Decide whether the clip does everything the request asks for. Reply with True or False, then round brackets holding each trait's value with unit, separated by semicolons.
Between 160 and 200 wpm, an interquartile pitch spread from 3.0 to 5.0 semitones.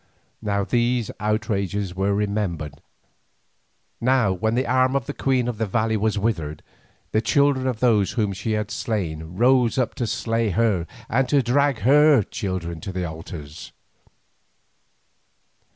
False (145 wpm; 4.4 semitones)